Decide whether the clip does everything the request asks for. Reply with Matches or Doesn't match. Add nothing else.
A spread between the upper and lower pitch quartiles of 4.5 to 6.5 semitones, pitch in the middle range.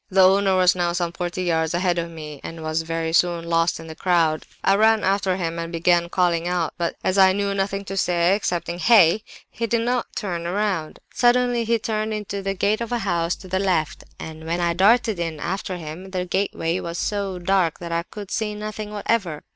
Doesn't match